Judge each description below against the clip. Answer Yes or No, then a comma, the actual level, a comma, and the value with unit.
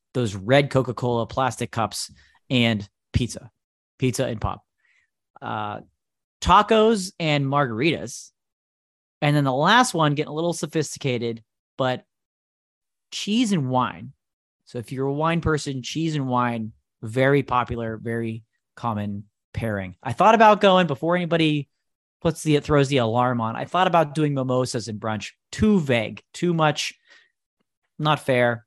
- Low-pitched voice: Yes, low, 130 Hz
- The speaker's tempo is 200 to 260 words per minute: No, average, 140 wpm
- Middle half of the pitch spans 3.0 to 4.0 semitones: No, wide, 5.6 semitones